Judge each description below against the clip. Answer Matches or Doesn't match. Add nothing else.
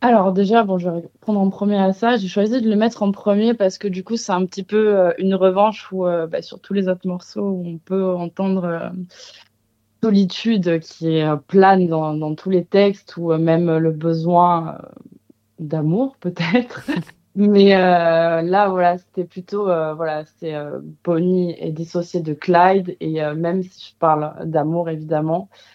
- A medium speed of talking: Matches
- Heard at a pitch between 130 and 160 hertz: Doesn't match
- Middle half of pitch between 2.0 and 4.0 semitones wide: Matches